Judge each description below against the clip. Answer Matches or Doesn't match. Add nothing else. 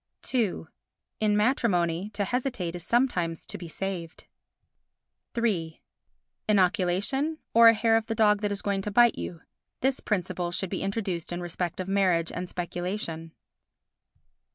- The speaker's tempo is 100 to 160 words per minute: Matches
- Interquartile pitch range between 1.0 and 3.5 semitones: Doesn't match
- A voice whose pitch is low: Doesn't match